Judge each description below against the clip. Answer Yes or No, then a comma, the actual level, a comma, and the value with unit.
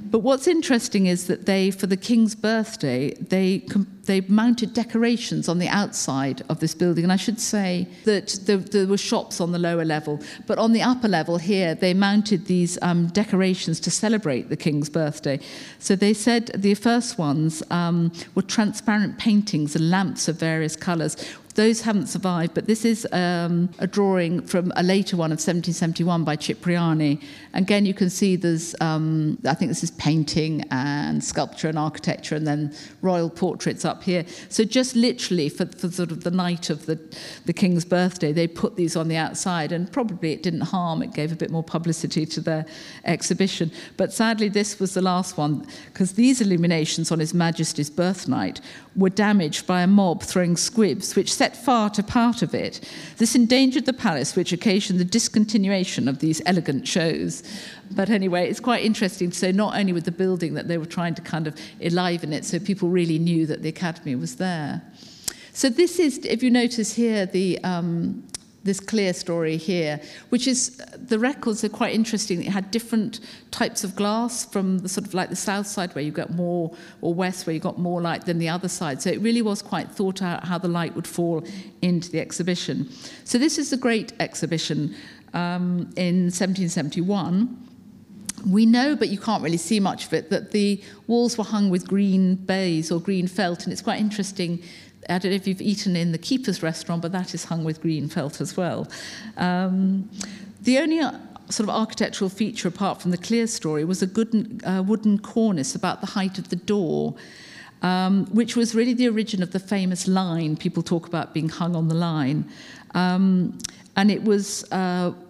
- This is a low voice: No, medium, 185 Hz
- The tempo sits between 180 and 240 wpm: Yes, average, 195 wpm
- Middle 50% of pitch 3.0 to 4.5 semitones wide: Yes, average, 3.8 semitones